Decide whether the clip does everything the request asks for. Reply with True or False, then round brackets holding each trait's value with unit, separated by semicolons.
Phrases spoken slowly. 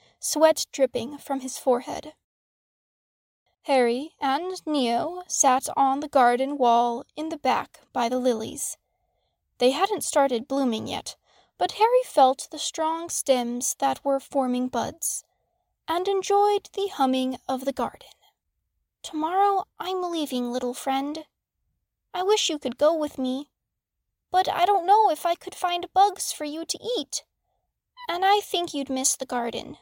False (145 wpm)